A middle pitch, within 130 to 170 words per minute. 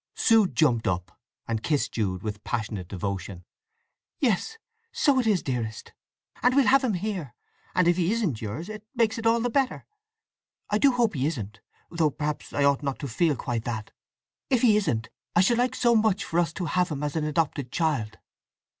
No: medium, 160 Hz; average, 190 wpm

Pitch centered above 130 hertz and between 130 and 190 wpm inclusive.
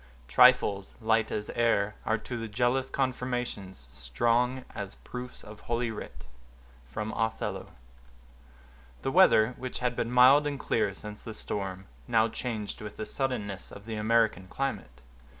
No: low, 115 Hz; average, 140 wpm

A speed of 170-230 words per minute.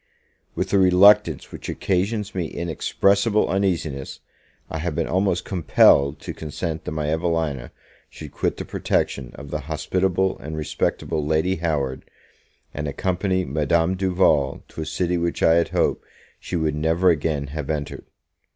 No: average, 150 wpm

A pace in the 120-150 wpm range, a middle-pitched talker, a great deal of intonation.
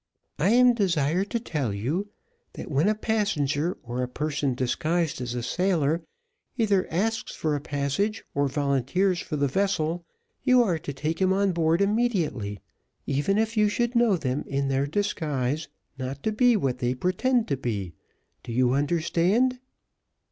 No: average, 160 wpm; medium, 165 Hz; wide, 6.6 semitones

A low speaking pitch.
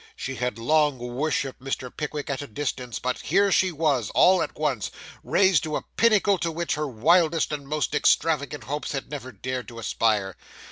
No: medium, 145 Hz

